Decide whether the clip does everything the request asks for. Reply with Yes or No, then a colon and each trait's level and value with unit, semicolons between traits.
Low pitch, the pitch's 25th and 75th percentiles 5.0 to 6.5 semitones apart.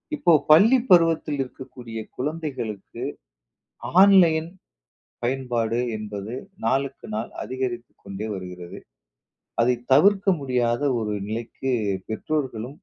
Yes: low, 125 Hz; wide, 5.5 semitones